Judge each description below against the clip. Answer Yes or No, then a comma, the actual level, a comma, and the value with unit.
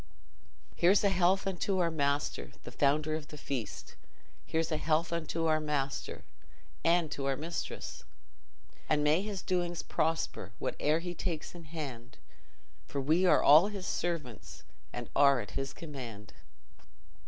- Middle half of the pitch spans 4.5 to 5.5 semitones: No, average, 3.4 semitones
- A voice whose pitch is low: No, medium, 155 Hz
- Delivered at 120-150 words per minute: Yes, average, 145 wpm